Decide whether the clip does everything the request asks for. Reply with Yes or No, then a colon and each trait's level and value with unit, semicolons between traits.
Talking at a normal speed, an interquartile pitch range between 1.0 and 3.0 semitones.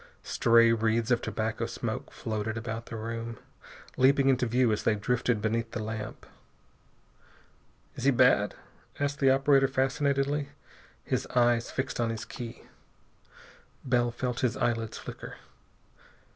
No: slow, 130 wpm; narrow, 2.6 semitones